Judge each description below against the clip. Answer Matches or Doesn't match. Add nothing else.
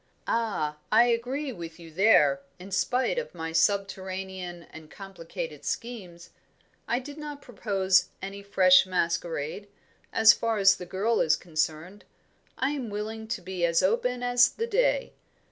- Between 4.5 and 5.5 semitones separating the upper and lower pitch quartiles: Matches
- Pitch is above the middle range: Matches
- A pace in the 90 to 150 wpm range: Matches